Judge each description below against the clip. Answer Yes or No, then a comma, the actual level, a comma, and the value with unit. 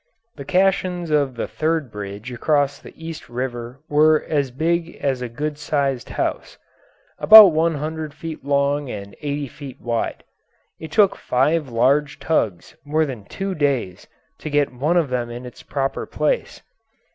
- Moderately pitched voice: Yes, medium, 145 Hz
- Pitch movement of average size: Yes, average, 4.0 semitones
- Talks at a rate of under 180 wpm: Yes, average, 160 wpm